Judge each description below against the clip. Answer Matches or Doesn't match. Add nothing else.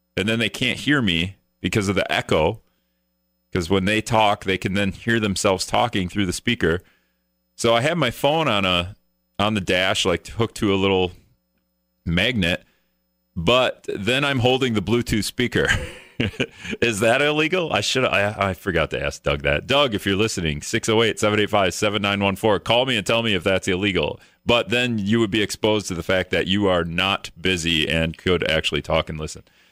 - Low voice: Matches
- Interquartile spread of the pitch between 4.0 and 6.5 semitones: Matches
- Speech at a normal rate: Matches